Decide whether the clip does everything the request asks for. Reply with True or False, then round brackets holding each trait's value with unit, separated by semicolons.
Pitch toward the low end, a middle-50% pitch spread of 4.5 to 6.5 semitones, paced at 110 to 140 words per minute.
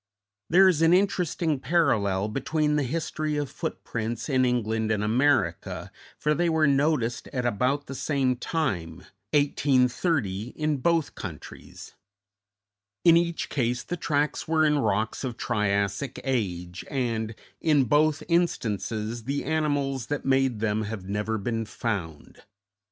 True (130 Hz; 5.6 semitones; 135 wpm)